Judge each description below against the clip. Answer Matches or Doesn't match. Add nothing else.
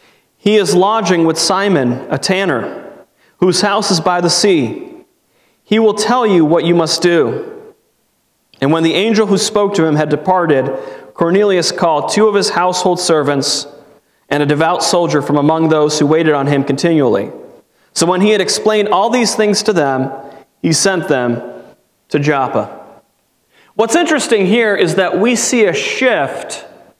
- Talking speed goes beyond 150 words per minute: Matches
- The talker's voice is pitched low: Doesn't match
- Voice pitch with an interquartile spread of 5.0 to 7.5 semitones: Matches